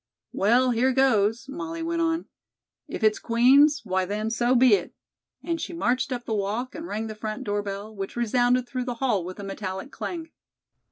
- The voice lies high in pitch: Yes, high, 240 Hz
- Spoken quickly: No, average, 190 wpm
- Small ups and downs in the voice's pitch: No, average, 4.2 semitones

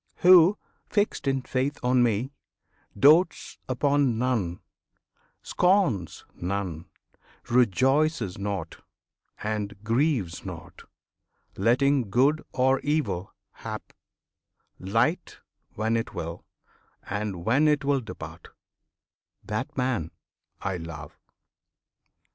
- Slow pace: Yes, slow, 90 wpm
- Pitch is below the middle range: Yes, low, 120 Hz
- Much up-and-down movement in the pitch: Yes, wide, 6.1 semitones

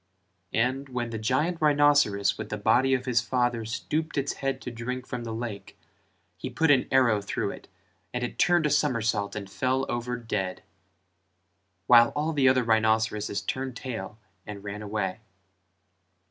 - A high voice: No, low, 120 Hz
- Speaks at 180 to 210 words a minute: No, average, 160 wpm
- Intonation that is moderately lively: Yes, average, 3.5 semitones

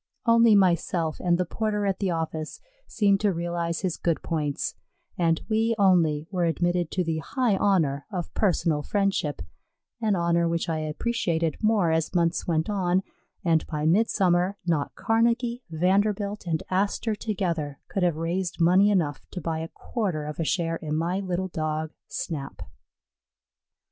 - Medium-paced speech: Yes, average, 155 wpm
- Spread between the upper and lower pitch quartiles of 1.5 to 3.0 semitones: No, average, 3.6 semitones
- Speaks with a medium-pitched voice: Yes, medium, 175 Hz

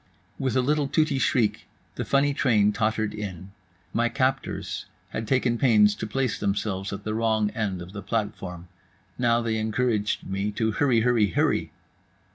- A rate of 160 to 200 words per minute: No, average, 150 wpm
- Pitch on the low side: Yes, low, 110 Hz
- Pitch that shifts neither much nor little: Yes, average, 3.4 semitones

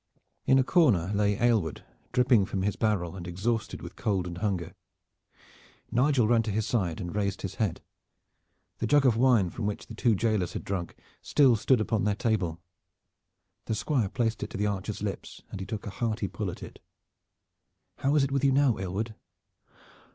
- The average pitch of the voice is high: No, low, 110 Hz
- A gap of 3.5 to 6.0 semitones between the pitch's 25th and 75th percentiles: Yes, average, 3.8 semitones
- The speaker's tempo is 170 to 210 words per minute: Yes, average, 190 wpm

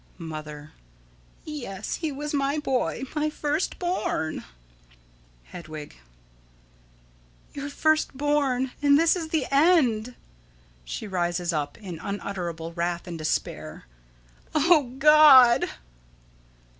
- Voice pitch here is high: Yes, very high, 255 Hz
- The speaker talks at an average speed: No, slow, 100 wpm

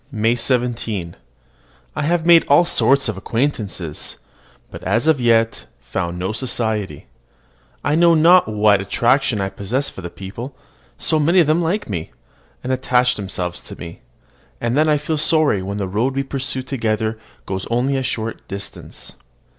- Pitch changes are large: Yes, wide, 5.8 semitones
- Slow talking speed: No, average, 160 wpm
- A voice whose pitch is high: No, low, 120 Hz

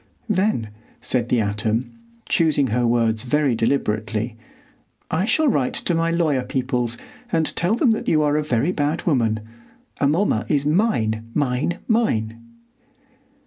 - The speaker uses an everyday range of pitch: No, wide, 6.2 semitones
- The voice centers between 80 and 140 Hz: Yes, low, 135 Hz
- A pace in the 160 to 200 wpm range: No, average, 140 wpm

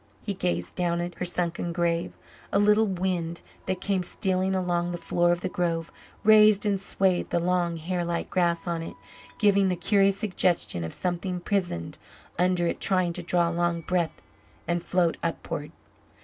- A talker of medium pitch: Yes, medium, 175 Hz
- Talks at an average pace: Yes, average, 175 wpm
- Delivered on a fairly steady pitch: Yes, narrow, 1.8 semitones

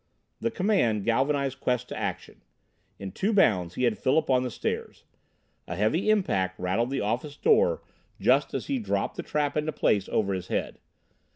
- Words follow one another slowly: No, average, 175 wpm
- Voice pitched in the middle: No, low, 130 Hz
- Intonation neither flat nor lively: No, wide, 8.0 semitones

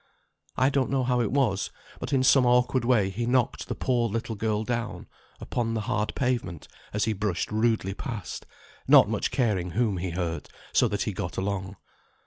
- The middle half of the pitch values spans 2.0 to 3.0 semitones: No, average, 3.8 semitones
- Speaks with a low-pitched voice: Yes, low, 115 Hz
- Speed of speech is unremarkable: Yes, average, 185 wpm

